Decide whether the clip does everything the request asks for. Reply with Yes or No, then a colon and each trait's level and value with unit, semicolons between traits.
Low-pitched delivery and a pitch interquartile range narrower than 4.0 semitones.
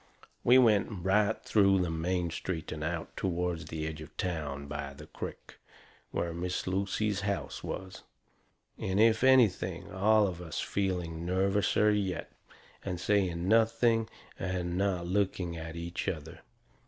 Yes: very low, 90 Hz; average, 3.2 semitones